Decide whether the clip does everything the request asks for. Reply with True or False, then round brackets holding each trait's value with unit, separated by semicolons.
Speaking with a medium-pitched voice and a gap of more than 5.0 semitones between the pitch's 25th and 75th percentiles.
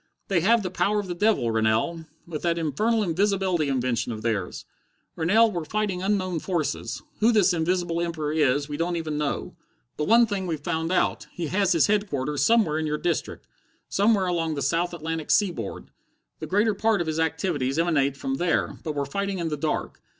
False (170 Hz; 4.4 semitones)